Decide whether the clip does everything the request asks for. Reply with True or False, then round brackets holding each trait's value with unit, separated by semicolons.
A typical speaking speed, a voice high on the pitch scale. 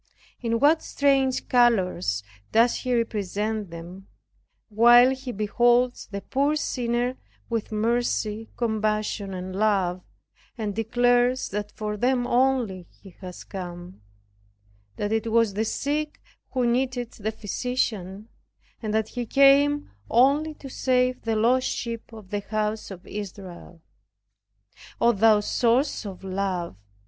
False (125 wpm; 225 Hz)